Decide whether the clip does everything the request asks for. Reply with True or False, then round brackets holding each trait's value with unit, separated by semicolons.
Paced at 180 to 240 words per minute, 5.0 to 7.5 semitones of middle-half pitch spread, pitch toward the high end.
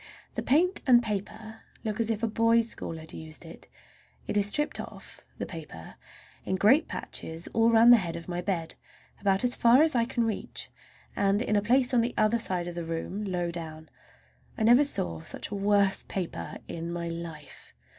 True (190 wpm; 5.3 semitones; 205 Hz)